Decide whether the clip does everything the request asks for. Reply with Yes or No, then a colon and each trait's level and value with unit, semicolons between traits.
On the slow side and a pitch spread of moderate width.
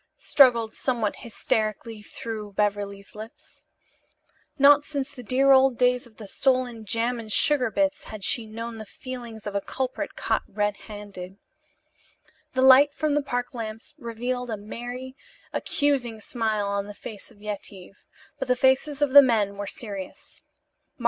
No: average, 155 wpm; average, 3.6 semitones